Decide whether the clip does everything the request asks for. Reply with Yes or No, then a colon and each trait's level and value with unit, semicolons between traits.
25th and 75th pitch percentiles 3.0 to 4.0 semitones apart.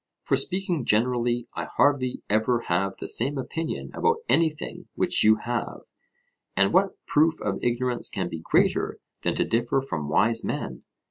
No: average, 5.3 semitones